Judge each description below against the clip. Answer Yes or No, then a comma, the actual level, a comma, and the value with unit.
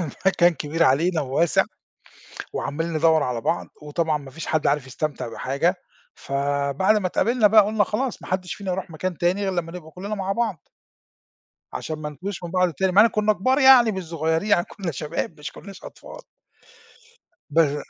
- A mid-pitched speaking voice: Yes, medium, 170 Hz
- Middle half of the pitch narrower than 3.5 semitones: No, average, 4.5 semitones